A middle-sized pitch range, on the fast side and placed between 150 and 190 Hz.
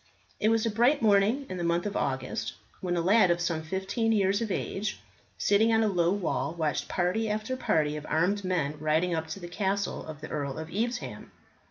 Yes: average, 4.9 semitones; fast, 210 wpm; medium, 185 Hz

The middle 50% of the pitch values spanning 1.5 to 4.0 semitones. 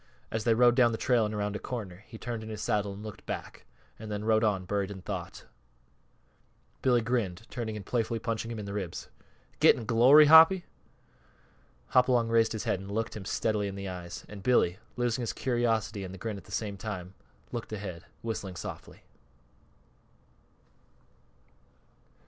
Yes: average, 2.8 semitones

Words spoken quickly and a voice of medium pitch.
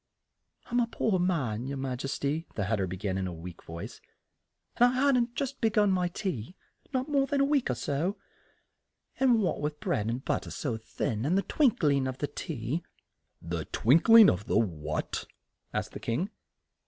Yes: fast, 210 wpm; medium, 145 Hz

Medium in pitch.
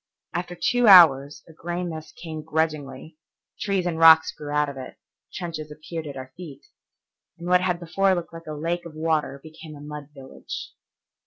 Yes: medium, 160 Hz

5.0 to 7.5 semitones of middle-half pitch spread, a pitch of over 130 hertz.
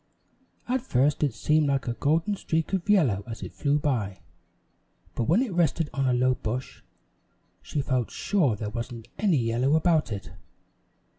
Yes: wide, 5.5 semitones; medium, 140 Hz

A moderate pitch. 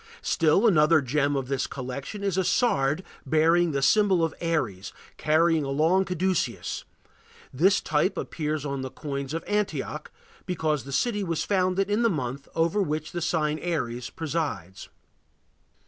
Yes: medium, 160 Hz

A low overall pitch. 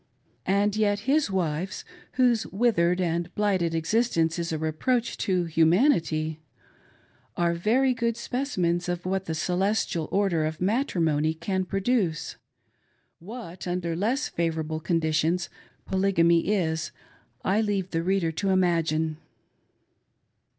No: medium, 180 Hz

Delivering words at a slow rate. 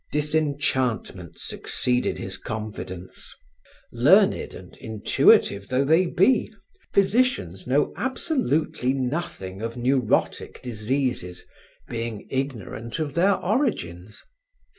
Yes: slow, 90 wpm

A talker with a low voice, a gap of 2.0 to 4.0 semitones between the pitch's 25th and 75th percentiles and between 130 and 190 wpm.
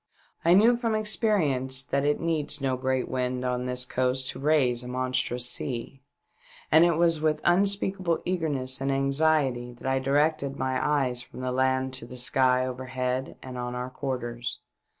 Yes: low, 130 Hz; average, 3.4 semitones; average, 170 wpm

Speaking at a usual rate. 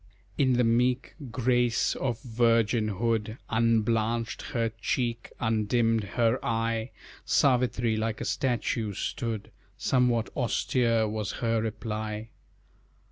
No: slow, 100 wpm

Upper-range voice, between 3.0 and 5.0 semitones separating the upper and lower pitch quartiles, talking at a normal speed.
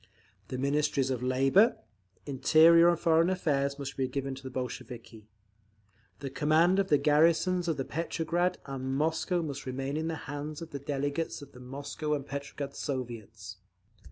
No: medium, 140 Hz; average, 3.4 semitones; average, 155 wpm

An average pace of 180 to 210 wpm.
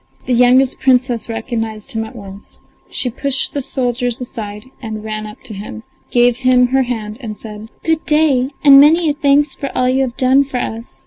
Yes: average, 190 wpm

